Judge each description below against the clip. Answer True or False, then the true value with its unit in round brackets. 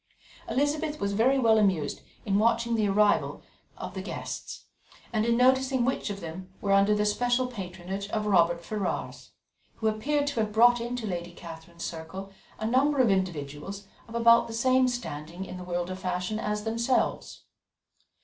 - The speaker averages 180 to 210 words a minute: False (170 wpm)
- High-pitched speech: True (210 Hz)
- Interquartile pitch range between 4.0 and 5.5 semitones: True (4.6 semitones)